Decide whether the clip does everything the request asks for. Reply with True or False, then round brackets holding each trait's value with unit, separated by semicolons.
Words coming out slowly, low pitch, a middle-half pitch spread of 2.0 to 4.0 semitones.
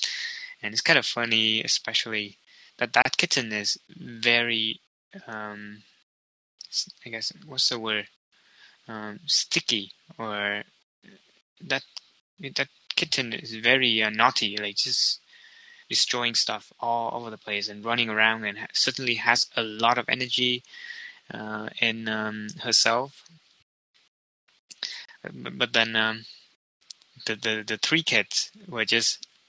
True (125 wpm; 115 Hz; 2.5 semitones)